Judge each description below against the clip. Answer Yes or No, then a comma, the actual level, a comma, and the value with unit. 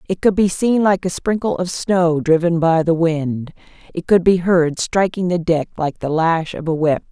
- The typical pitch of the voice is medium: Yes, medium, 170 Hz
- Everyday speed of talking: No, fast, 220 wpm